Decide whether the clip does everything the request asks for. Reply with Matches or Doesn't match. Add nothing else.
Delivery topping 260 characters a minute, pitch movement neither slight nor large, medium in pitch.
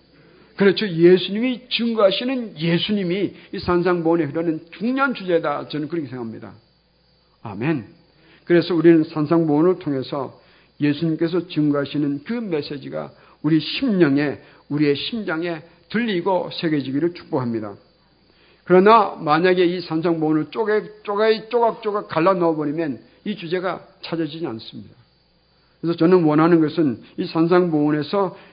Matches